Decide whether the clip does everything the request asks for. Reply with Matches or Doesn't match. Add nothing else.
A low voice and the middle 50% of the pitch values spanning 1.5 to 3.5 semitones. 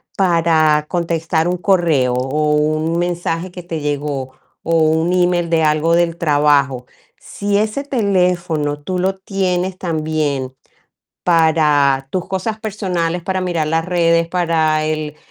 Doesn't match